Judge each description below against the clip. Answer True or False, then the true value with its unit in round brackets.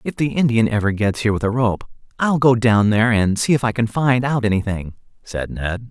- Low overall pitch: True (115 Hz)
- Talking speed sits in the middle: False (235 wpm)